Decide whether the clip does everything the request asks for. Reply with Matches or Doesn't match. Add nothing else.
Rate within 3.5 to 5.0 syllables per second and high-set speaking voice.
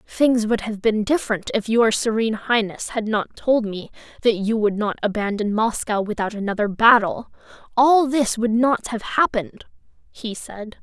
Matches